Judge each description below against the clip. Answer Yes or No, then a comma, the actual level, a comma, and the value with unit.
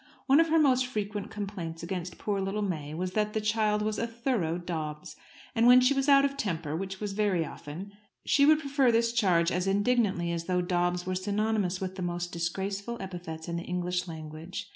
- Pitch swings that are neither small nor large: Yes, average, 4.2 semitones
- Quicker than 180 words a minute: Yes, fast, 205 wpm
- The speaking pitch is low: No, high, 195 Hz